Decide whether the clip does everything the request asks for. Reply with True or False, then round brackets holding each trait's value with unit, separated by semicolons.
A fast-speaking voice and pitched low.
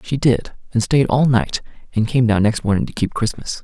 True (230 wpm; 120 Hz)